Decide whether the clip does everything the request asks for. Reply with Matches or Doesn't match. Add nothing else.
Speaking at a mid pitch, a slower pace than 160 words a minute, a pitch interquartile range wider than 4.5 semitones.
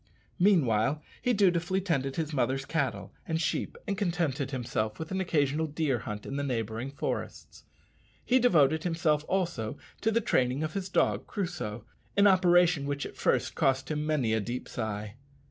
Doesn't match